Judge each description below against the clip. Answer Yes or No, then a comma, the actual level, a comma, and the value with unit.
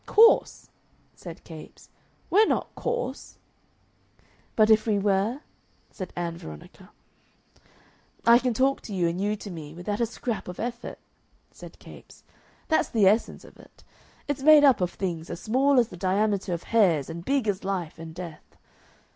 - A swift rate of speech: No, average, 165 wpm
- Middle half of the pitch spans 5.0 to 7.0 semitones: Yes, wide, 5.4 semitones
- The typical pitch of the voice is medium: No, high, 205 Hz